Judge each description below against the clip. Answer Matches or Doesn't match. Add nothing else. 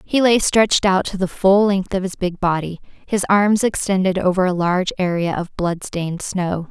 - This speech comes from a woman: Matches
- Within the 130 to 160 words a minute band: Doesn't match